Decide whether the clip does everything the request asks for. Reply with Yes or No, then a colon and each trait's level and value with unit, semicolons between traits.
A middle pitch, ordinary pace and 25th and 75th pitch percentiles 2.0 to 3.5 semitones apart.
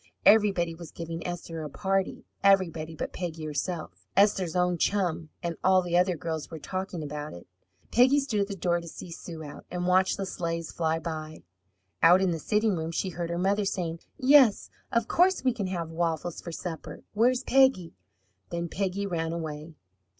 Yes: medium, 175 Hz; average, 185 wpm; average, 3.1 semitones